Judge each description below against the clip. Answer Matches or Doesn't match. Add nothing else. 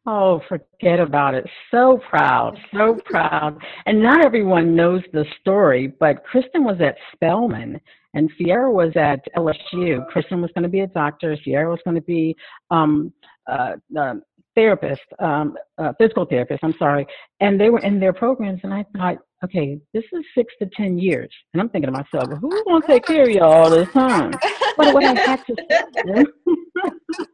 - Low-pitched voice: Doesn't match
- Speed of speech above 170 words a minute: Matches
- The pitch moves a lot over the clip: Matches